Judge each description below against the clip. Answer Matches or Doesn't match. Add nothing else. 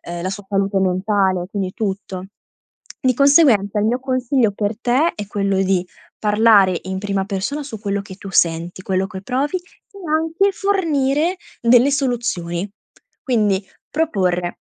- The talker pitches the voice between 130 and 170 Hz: Doesn't match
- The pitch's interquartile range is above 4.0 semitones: Matches